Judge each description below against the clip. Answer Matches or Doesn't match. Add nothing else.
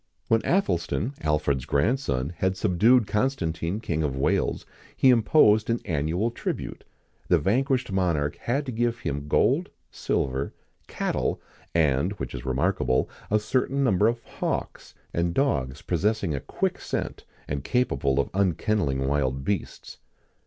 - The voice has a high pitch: Doesn't match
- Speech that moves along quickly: Doesn't match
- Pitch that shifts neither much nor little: Doesn't match